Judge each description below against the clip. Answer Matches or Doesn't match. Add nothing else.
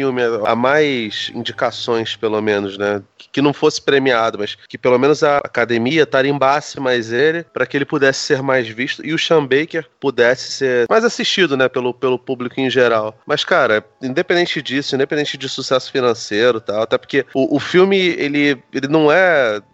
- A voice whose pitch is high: Doesn't match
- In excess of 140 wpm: Matches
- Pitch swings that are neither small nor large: Matches